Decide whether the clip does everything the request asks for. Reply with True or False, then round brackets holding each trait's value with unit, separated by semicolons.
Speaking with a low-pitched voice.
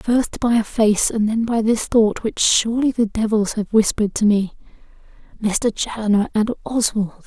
False (220 Hz)